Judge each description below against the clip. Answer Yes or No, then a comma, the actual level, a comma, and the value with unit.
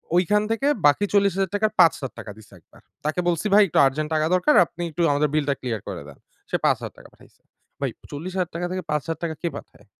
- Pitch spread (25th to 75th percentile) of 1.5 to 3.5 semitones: No, average, 4.5 semitones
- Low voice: No, medium, 165 Hz